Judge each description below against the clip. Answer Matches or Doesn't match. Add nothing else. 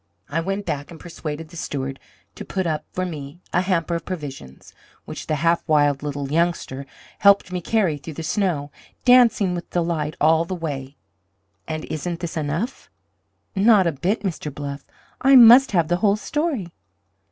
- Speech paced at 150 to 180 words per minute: Matches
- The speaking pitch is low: Doesn't match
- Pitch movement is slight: Doesn't match